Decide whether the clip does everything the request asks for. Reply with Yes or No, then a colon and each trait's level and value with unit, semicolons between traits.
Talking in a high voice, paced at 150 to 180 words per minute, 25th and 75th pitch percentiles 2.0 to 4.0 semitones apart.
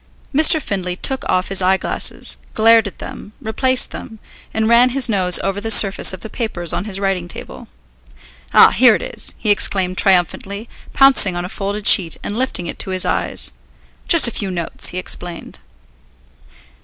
Yes: high, 200 Hz; average, 175 wpm; average, 3.6 semitones